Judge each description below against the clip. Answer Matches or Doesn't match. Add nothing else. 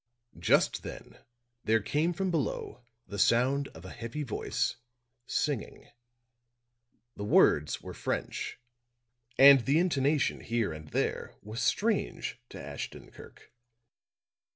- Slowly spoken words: Matches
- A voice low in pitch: Matches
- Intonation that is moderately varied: Doesn't match